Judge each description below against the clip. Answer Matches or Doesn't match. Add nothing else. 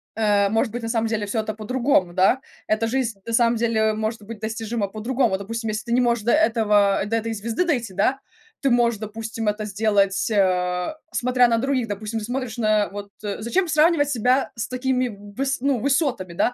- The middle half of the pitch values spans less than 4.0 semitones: Matches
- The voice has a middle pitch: Doesn't match